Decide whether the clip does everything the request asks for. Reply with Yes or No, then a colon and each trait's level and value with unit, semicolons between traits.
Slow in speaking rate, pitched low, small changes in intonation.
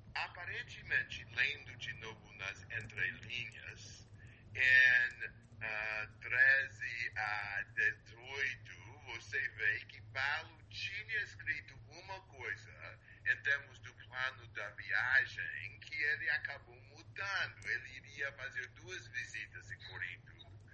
Yes: slow, 105 wpm; low, 110 Hz; narrow, 1.5 semitones